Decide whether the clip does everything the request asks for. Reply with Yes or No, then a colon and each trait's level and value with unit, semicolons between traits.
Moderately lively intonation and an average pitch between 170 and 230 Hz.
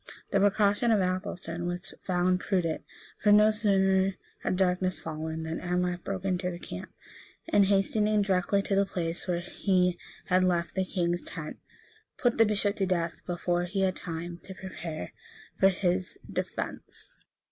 No: narrow, 2.0 semitones; medium, 185 Hz